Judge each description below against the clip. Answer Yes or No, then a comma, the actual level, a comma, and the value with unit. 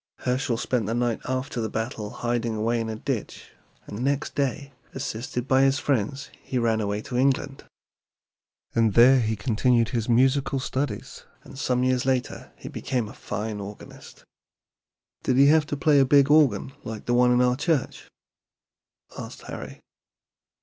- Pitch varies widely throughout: No, average, 3.1 semitones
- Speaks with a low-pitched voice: Yes, low, 125 Hz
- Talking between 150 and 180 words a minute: Yes, average, 160 wpm